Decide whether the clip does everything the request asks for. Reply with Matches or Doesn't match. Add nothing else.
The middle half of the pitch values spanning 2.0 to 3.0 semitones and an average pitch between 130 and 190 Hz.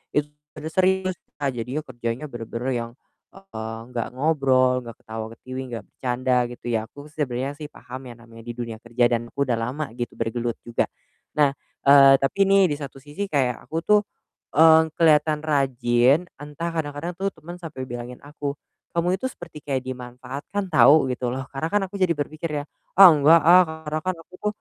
Doesn't match